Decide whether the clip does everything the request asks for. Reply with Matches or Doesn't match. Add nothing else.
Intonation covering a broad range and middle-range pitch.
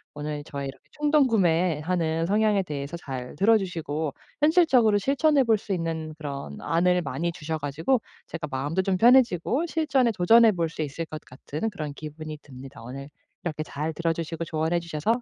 Matches